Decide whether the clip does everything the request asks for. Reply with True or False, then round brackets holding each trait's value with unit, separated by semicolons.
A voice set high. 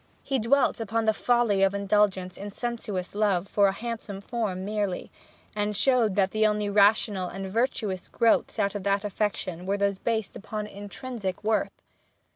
True (205 Hz)